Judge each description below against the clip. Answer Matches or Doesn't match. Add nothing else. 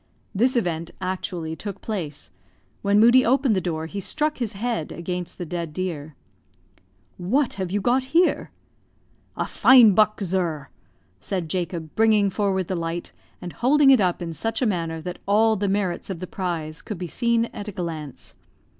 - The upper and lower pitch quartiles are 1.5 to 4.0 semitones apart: Doesn't match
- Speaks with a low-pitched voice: Doesn't match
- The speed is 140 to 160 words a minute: Doesn't match